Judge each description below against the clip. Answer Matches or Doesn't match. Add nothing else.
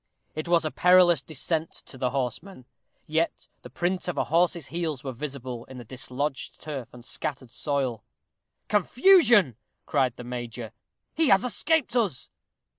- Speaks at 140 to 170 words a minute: Matches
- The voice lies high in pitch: Doesn't match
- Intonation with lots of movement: Matches